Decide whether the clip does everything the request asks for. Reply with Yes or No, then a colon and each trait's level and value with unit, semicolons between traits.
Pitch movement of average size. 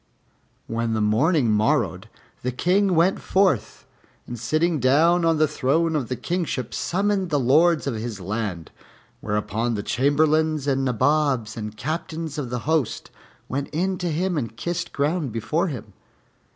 No: wide, 6.2 semitones